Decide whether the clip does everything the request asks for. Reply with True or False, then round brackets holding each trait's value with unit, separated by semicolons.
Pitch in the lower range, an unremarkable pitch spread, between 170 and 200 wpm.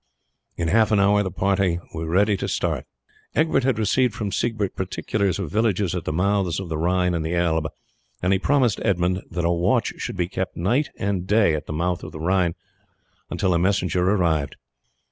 True (95 Hz; 3.0 semitones; 195 wpm)